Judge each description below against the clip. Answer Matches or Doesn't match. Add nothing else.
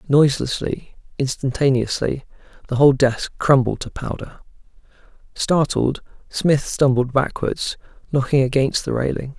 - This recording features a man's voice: Matches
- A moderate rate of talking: Doesn't match